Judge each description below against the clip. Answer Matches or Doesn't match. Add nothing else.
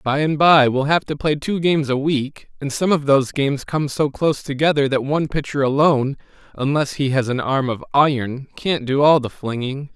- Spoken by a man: Matches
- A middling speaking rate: Doesn't match